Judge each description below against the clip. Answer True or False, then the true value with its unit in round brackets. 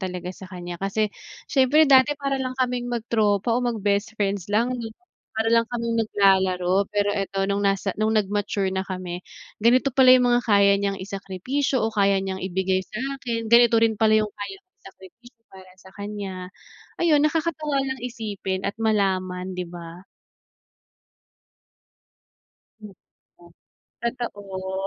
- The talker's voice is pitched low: False (205 Hz)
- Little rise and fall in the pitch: False (4.1 semitones)